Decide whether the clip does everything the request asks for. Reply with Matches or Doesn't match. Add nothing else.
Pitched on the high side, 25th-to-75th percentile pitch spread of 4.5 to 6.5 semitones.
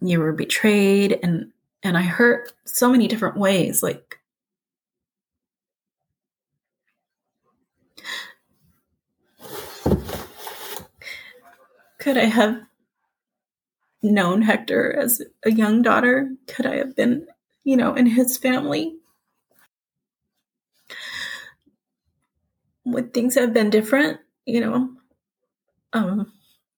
Doesn't match